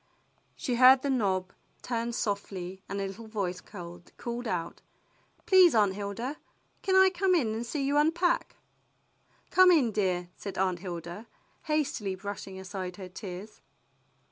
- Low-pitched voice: No, high, 210 Hz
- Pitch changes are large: Yes, wide, 6.0 semitones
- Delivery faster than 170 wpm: No, average, 150 wpm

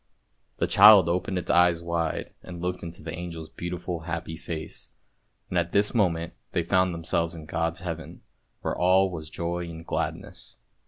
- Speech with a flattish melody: Yes, narrow, 1.5 semitones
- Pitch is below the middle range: Yes, very low, 85 Hz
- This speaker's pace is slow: No, average, 170 wpm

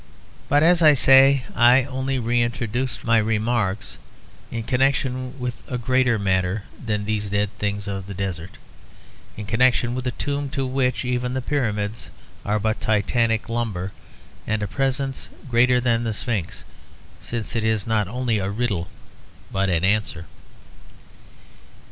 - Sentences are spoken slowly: No, average, 145 wpm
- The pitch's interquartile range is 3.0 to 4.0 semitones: Yes, average, 3.7 semitones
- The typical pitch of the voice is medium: No, low, 115 Hz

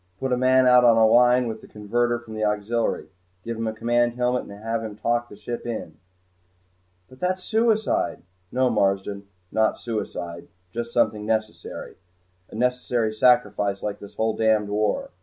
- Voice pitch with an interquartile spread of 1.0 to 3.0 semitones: Yes, narrow, 2.6 semitones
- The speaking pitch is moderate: No, low, 115 Hz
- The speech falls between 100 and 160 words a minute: No, average, 170 wpm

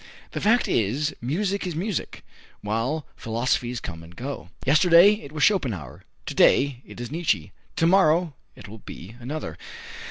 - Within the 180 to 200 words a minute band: No, average, 155 wpm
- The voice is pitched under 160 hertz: Yes, medium, 140 Hz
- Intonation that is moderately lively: No, wide, 7.0 semitones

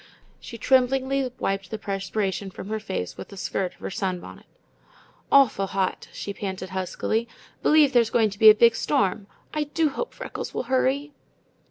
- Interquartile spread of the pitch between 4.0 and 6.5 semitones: Yes, average, 5.2 semitones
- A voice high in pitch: Yes, high, 220 Hz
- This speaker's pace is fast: No, average, 170 wpm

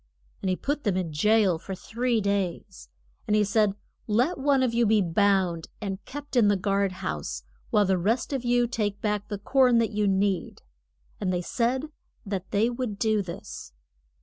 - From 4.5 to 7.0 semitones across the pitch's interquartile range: No, average, 3.6 semitones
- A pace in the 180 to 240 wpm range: Yes, average, 185 wpm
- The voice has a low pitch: No, high, 205 Hz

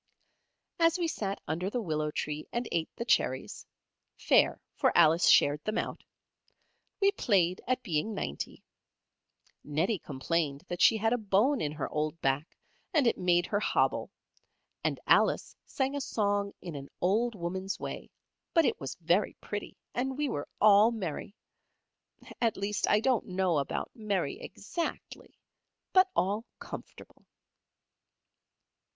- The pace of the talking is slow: No, average, 145 wpm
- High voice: Yes, high, 200 Hz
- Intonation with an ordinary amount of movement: No, wide, 6.3 semitones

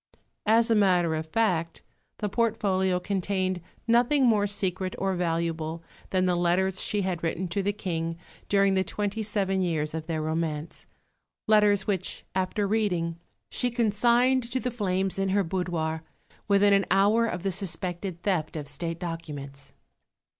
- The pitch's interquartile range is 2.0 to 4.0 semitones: Yes, average, 3.5 semitones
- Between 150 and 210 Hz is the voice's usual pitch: Yes, high, 190 Hz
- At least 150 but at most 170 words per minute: Yes, average, 155 wpm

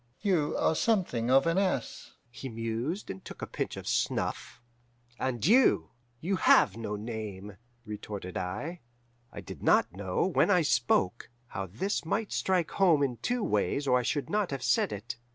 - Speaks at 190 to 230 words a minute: No, average, 170 wpm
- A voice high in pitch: No, low, 130 Hz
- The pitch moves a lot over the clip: Yes, wide, 8.9 semitones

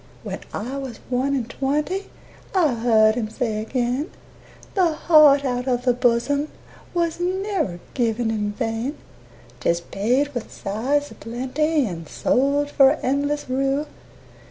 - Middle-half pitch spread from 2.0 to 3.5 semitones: No, average, 3.9 semitones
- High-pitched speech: Yes, very high, 260 Hz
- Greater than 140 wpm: No, slow, 135 wpm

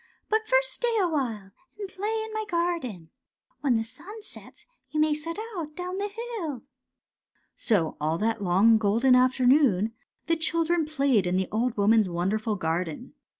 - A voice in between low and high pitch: No, very high, 265 Hz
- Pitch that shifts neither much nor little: No, wide, 8.7 semitones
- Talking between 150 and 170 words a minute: Yes, average, 165 wpm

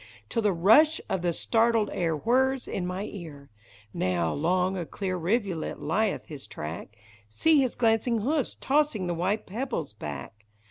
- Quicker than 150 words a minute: Yes, average, 165 wpm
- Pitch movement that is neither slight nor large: No, wide, 6.6 semitones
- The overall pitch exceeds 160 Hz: Yes, high, 190 Hz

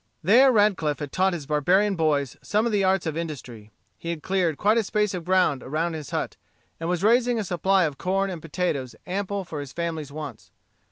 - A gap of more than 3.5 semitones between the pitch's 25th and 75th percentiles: Yes, average, 4.3 semitones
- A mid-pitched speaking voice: Yes, medium, 175 Hz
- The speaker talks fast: Yes, fast, 210 wpm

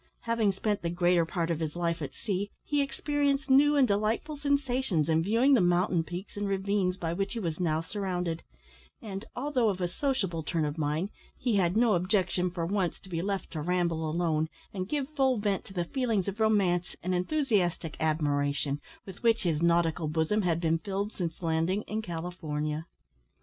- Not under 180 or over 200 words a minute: Yes, average, 185 wpm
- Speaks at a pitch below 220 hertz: Yes, medium, 185 Hz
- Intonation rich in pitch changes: No, average, 4.5 semitones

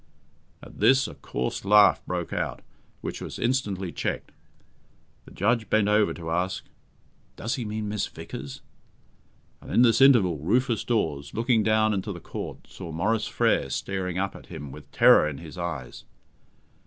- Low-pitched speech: Yes, low, 100 Hz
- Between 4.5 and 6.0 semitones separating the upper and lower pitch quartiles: Yes, average, 4.8 semitones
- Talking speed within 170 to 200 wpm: No, average, 160 wpm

